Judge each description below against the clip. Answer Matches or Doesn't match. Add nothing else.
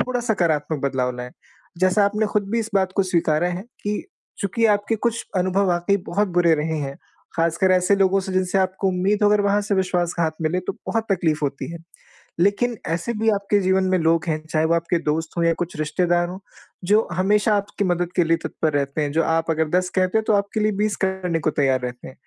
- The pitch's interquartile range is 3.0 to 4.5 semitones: Matches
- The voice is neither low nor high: Matches